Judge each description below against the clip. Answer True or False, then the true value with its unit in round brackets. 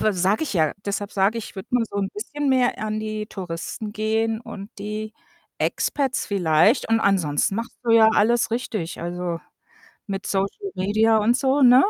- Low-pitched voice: False (215 Hz)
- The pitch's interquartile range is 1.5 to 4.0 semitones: True (2.9 semitones)